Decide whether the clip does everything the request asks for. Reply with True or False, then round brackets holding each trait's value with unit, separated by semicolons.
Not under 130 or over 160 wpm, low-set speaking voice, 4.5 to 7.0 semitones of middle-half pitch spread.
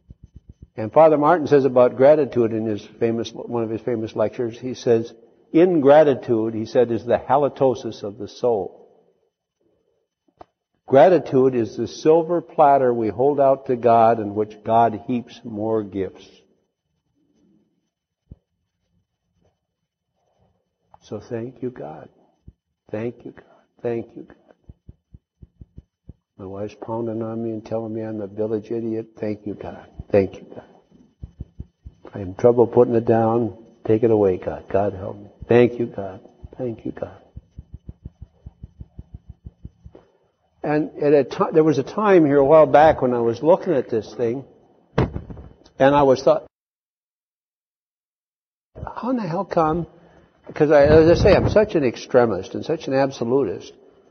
True (145 wpm; 120 Hz; 4.9 semitones)